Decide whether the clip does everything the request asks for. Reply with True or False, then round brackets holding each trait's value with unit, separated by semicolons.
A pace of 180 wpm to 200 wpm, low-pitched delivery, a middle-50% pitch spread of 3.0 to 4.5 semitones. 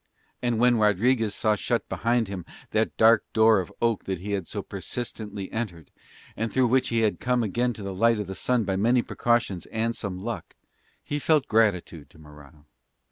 True (190 wpm; 110 Hz; 3.6 semitones)